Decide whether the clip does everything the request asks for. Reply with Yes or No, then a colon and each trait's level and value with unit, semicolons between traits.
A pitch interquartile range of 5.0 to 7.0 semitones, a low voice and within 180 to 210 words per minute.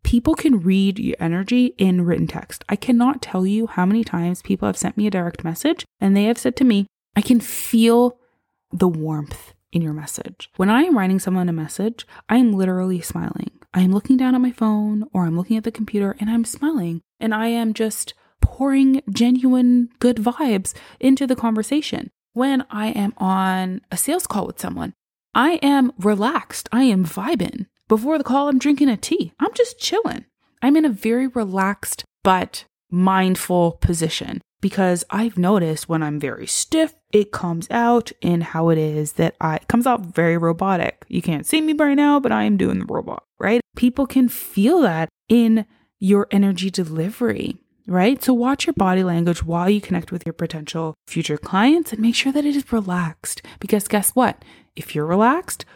No: wide, 5.5 semitones; high, 215 Hz; average, 190 wpm